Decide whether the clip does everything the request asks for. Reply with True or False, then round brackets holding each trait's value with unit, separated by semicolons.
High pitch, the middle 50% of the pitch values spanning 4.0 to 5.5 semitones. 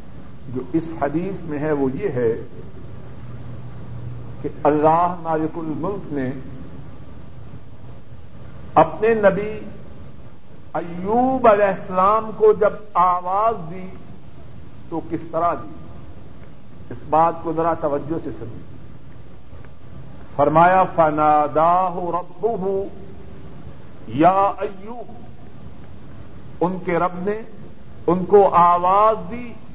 False (170 Hz; 4.7 semitones)